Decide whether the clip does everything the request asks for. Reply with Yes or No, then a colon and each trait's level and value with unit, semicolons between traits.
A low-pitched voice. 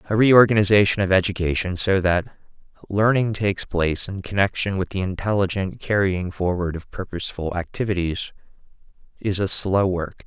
Yes: very low, 95 Hz